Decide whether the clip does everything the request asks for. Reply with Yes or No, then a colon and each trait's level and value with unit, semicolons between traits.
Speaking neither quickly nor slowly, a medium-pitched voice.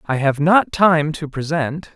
Yes: average, 185 wpm; medium, 155 Hz